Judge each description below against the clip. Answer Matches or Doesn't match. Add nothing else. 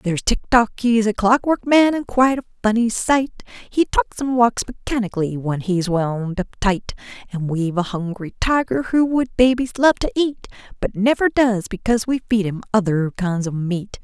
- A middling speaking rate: Matches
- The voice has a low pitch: Doesn't match